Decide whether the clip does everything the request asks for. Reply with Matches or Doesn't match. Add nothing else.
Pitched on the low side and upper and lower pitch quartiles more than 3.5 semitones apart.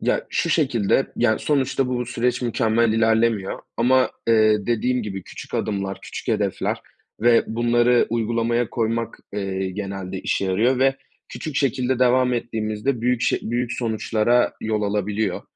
Doesn't match